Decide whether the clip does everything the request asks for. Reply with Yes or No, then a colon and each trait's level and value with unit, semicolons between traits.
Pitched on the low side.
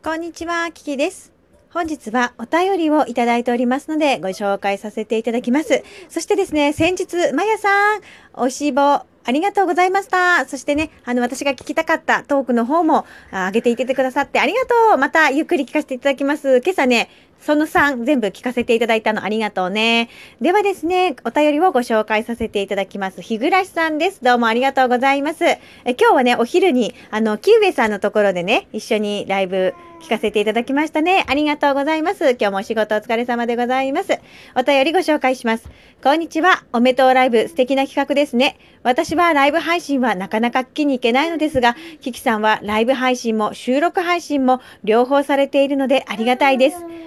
No: very high, 270 Hz